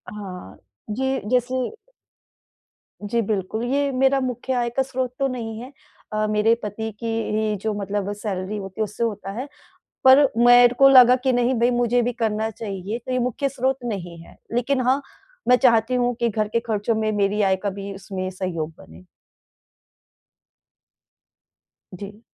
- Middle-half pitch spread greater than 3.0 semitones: Yes, average, 3.5 semitones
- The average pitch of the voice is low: No, high, 225 Hz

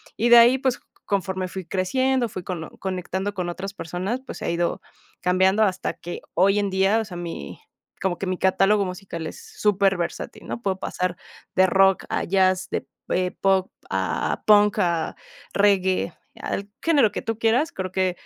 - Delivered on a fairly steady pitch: Yes, narrow, 2.2 semitones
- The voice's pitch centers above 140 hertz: Yes, high, 190 Hz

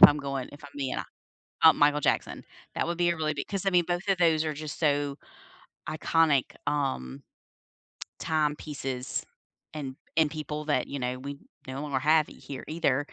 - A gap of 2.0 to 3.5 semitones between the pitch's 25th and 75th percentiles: Yes, narrow, 2.4 semitones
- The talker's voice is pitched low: No, medium, 150 Hz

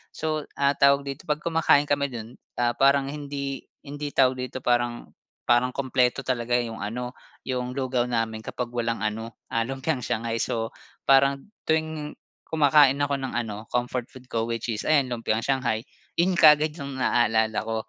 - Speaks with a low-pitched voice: Yes, low, 130 Hz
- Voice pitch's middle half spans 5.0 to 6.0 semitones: No, average, 3.2 semitones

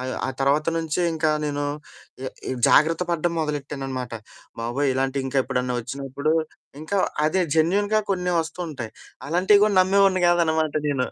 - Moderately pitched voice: Yes, medium, 155 Hz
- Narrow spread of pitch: No, average, 4.4 semitones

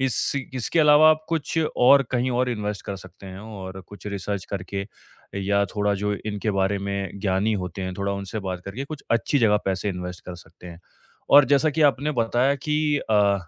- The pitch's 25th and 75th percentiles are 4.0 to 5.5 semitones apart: Yes, average, 5.2 semitones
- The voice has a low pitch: Yes, low, 105 Hz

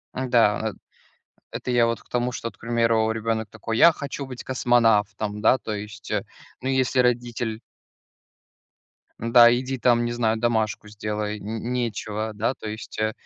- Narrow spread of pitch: Yes, narrow, 2.1 semitones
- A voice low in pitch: Yes, low, 115 Hz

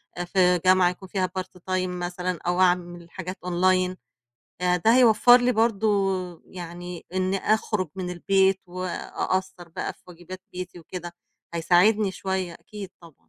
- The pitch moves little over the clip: Yes, narrow, 1.3 semitones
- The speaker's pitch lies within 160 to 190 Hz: Yes, medium, 185 Hz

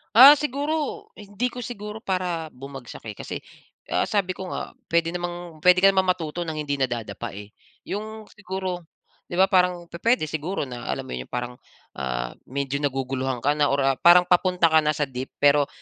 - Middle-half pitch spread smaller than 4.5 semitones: No, wide, 5.6 semitones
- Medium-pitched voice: Yes, medium, 165 Hz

